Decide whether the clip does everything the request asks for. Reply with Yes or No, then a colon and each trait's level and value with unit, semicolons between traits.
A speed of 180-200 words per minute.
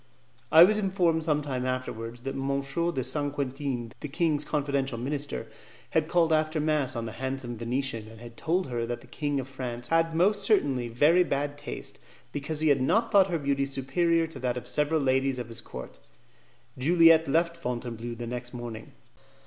Yes: average, 185 wpm